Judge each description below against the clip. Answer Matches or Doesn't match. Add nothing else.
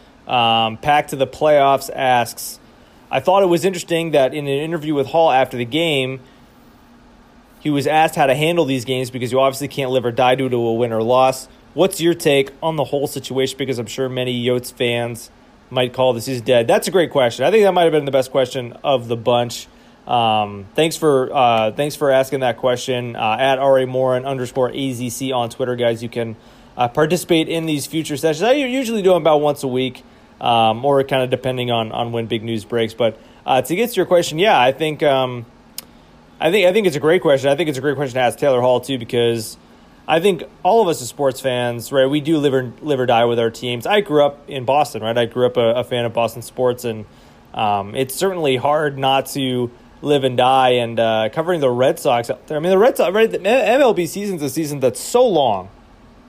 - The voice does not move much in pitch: Doesn't match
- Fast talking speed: Matches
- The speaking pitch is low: Matches